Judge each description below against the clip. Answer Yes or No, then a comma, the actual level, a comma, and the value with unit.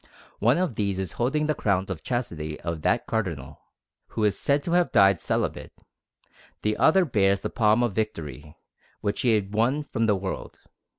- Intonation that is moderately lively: Yes, average, 4.5 semitones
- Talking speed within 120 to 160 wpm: No, average, 180 wpm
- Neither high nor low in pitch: No, low, 105 Hz